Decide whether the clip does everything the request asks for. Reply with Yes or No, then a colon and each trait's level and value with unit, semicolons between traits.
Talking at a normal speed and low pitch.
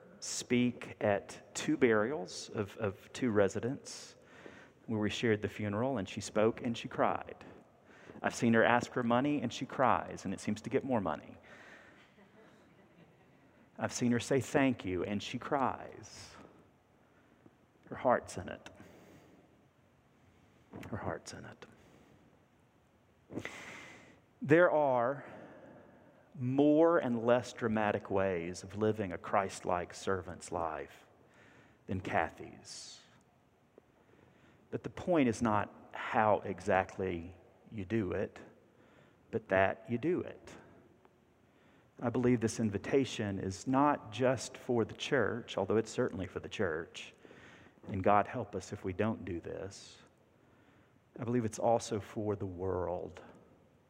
No: slow, 130 wpm; low, 110 Hz